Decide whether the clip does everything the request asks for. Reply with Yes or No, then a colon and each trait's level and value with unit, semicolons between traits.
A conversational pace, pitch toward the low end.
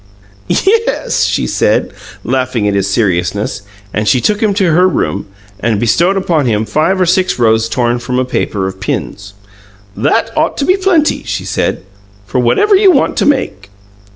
Yes: average, 175 wpm; low, 130 Hz